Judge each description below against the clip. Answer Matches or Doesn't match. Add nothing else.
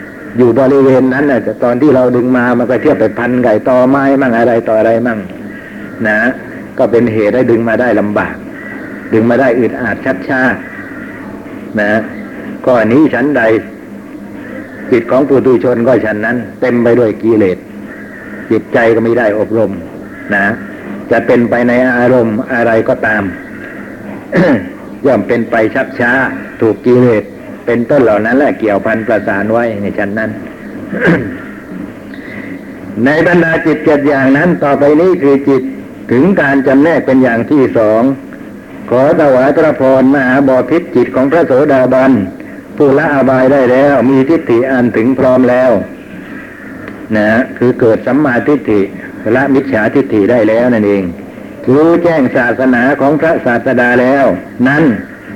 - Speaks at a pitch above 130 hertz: Doesn't match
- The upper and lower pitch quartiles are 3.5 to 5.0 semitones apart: Doesn't match